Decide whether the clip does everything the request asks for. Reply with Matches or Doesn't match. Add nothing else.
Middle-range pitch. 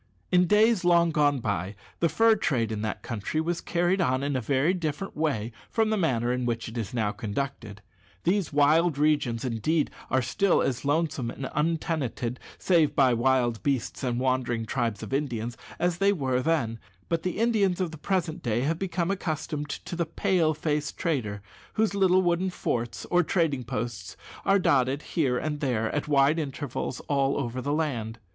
Matches